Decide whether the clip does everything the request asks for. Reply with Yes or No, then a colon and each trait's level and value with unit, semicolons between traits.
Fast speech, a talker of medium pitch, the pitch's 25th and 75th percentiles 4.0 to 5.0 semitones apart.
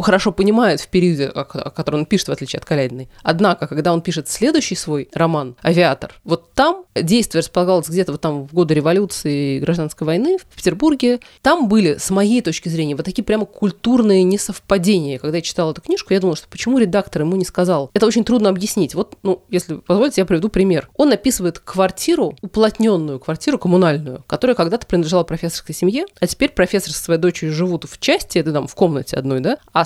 Yes: fast, 195 wpm; medium, 180 Hz; average, 4.7 semitones